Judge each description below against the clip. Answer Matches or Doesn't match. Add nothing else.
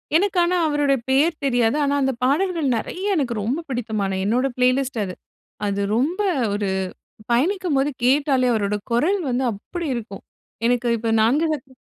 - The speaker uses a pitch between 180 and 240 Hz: Doesn't match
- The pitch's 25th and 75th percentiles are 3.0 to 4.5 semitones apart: Doesn't match